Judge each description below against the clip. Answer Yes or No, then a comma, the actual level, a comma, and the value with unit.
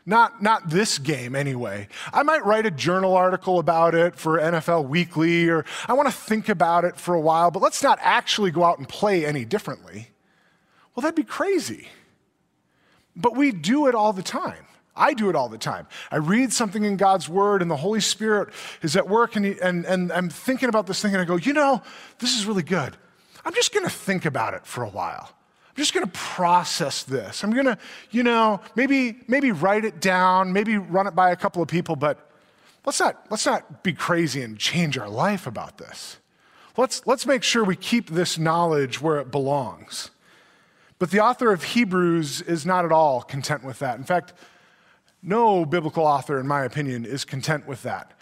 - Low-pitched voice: No, medium, 185 Hz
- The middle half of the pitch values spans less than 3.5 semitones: No, average, 5.3 semitones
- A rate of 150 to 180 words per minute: No, fast, 205 wpm